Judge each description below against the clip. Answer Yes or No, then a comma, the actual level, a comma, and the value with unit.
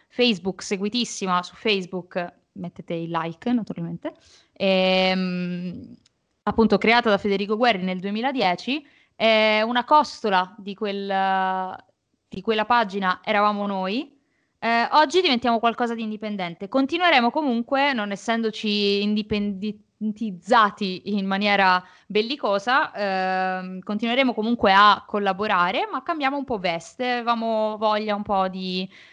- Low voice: No, high, 210 Hz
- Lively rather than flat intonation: No, average, 3.8 semitones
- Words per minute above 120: No, slow, 115 wpm